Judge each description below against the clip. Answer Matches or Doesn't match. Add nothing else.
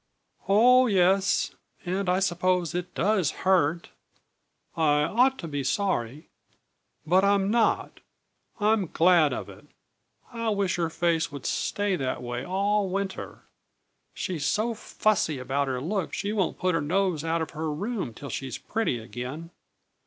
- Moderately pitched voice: Matches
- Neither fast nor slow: Matches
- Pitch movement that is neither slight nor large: Matches